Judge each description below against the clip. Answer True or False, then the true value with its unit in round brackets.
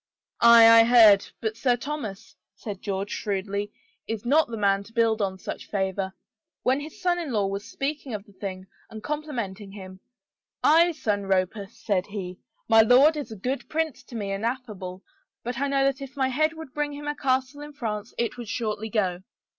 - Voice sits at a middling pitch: False (225 Hz)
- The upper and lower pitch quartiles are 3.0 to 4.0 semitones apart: False (5.5 semitones)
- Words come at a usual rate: False (210 wpm)